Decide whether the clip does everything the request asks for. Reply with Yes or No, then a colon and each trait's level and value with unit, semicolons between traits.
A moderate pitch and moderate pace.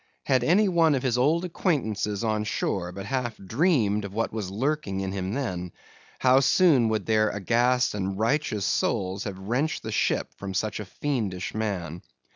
No: low, 110 Hz; average, 175 wpm